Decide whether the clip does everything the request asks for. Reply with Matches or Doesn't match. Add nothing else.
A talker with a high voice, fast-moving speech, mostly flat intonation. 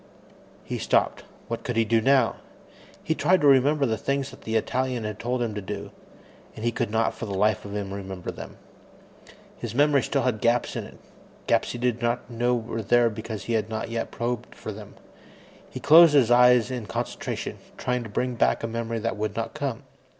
Doesn't match